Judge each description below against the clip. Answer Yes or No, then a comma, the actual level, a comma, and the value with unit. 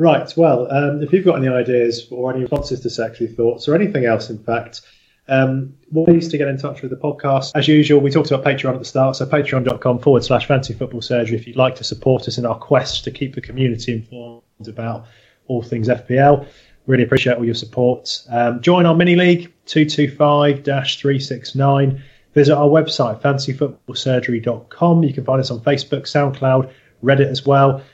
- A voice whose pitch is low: Yes, low, 130 Hz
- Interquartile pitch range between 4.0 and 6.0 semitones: No, average, 2.9 semitones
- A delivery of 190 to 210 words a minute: Yes, average, 195 wpm